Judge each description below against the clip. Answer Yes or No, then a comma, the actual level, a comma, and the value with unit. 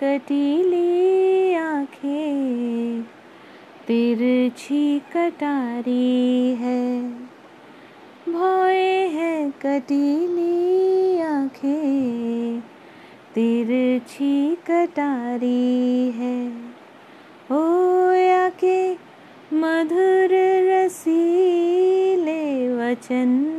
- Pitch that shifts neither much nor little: No, wide, 5.9 semitones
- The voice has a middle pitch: No, very high, 290 Hz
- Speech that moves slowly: Yes, slow, 45 wpm